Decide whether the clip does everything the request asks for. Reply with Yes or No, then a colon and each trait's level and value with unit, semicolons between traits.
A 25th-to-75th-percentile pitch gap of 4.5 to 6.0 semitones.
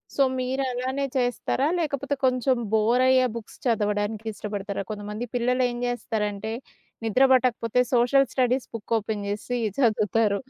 No: average, 3.3 semitones